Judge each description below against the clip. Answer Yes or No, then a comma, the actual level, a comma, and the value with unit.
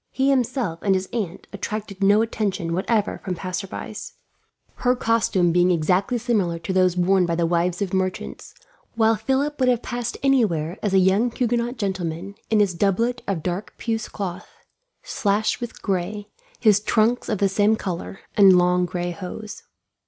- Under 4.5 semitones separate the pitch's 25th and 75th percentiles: Yes, average, 3.9 semitones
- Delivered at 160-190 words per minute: Yes, average, 165 wpm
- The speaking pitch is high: Yes, high, 200 Hz